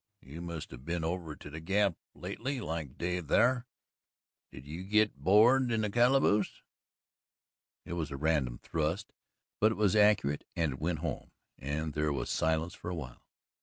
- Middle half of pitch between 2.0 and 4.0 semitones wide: No, wide, 5.6 semitones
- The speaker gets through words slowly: No, average, 170 wpm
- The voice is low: Yes, very low, 85 Hz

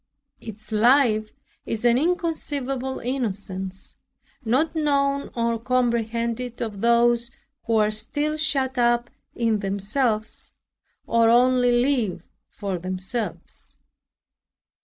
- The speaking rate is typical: No, slow, 95 wpm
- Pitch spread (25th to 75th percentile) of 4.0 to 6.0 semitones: No, average, 3.3 semitones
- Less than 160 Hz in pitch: No, high, 235 Hz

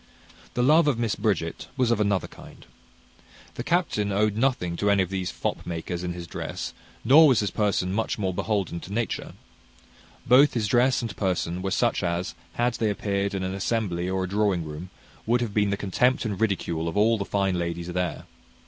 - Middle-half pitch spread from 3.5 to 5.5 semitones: Yes, average, 4.0 semitones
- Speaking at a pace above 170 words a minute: Yes, average, 200 wpm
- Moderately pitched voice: No, low, 100 Hz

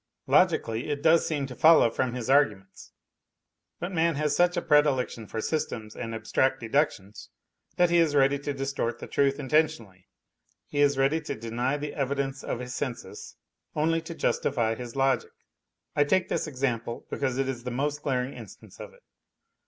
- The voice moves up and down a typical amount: Yes, average, 3.6 semitones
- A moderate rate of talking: Yes, average, 175 wpm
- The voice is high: No, low, 135 Hz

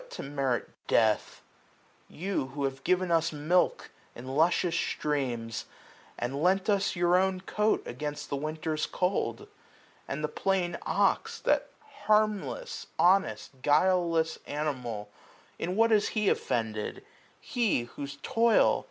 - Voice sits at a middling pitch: Yes, medium, 160 Hz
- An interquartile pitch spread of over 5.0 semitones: Yes, wide, 5.6 semitones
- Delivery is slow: Yes, slow, 125 wpm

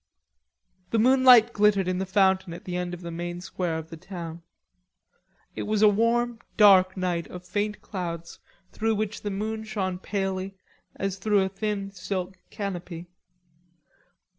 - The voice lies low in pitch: No, high, 190 Hz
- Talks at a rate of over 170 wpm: No, average, 155 wpm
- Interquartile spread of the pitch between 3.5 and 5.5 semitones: No, average, 2.8 semitones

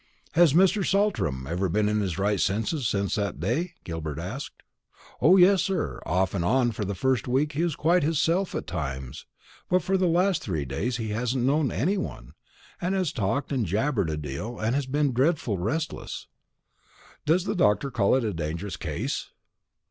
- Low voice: Yes, low, 120 Hz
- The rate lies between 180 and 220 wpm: Yes, average, 185 wpm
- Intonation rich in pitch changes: Yes, wide, 9.0 semitones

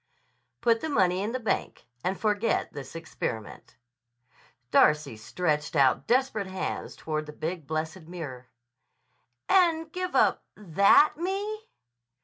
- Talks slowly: Yes, slow, 125 wpm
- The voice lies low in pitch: No, medium, 185 Hz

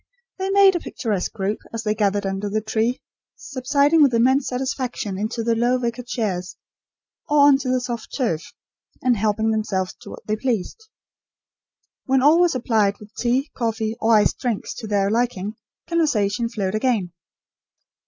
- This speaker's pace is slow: No, average, 165 wpm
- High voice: Yes, high, 230 Hz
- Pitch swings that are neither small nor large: Yes, average, 3.6 semitones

